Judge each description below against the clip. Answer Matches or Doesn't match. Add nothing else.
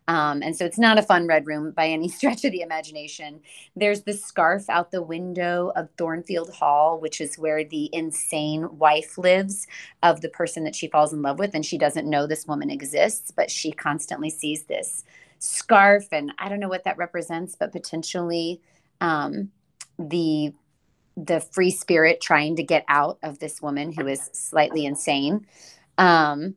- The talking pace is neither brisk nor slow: Matches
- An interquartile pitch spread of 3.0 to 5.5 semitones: Doesn't match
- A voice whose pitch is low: Doesn't match